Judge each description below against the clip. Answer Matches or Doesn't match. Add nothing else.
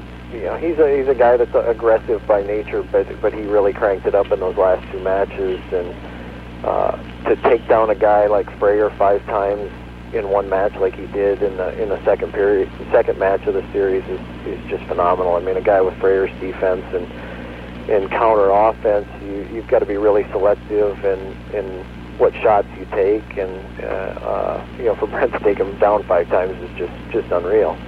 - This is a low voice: Matches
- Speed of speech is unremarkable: Doesn't match